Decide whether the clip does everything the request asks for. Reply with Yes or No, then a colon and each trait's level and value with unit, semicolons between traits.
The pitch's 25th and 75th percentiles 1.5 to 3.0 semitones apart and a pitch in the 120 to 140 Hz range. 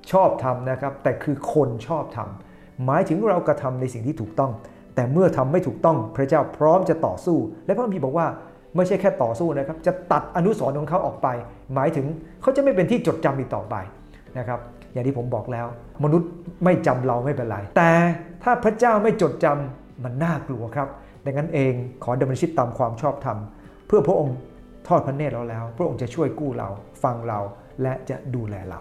No: wide, 5.6 semitones; low, 135 Hz